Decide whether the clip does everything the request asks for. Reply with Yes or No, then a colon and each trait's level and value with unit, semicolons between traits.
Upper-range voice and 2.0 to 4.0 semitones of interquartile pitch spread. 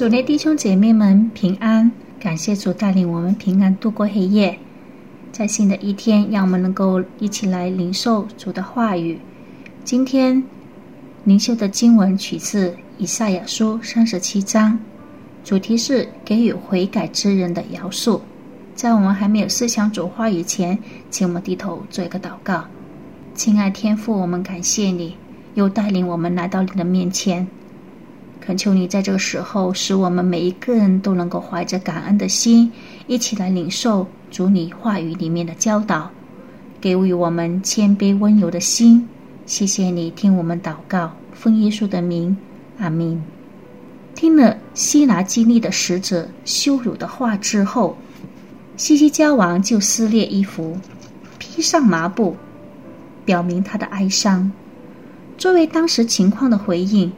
Yes: high, 200 Hz; average, 3.7 semitones